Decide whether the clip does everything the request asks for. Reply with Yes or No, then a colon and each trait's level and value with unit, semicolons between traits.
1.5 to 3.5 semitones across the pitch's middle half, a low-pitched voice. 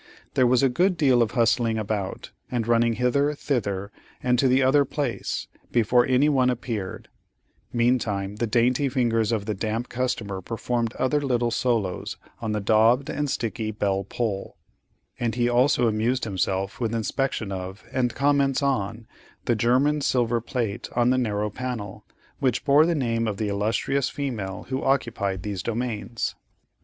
Yes: average, 3.2 semitones; low, 120 Hz